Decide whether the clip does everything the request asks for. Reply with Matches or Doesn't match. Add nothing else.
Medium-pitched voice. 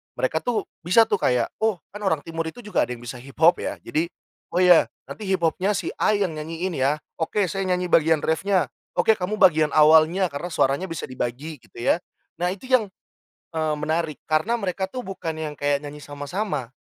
Matches